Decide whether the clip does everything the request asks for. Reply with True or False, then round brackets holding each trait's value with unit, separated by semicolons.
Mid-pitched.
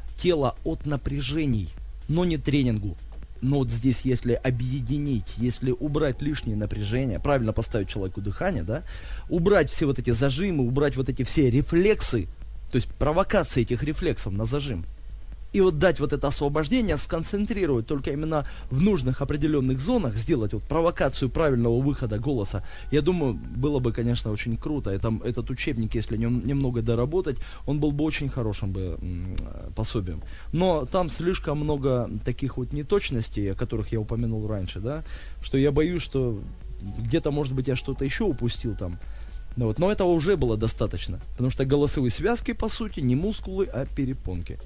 False (130 Hz)